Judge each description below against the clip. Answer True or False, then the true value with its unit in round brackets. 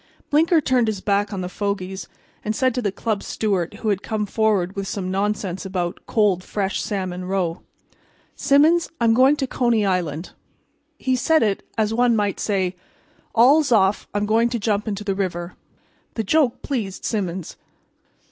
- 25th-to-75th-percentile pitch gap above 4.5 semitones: False (3.6 semitones)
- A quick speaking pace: False (165 wpm)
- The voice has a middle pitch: False (205 Hz)